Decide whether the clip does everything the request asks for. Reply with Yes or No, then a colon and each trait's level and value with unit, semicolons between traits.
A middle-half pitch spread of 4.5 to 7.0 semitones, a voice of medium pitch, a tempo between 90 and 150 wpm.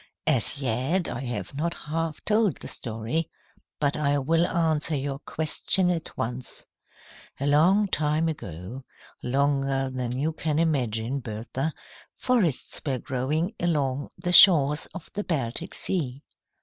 No: average, 4.1 semitones; medium, 145 Hz; slow, 135 wpm